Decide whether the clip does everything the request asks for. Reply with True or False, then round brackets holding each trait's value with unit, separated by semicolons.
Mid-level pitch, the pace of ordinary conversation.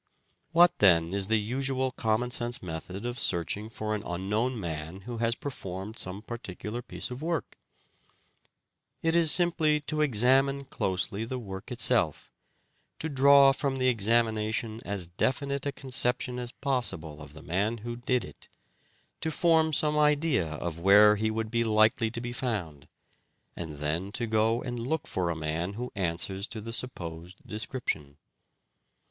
False (115 Hz; 155 wpm)